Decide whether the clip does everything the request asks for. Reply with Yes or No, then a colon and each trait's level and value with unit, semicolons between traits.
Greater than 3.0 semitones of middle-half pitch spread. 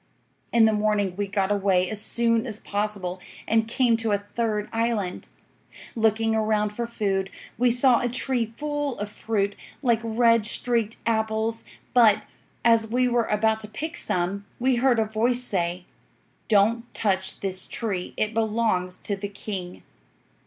No: narrow, 2.4 semitones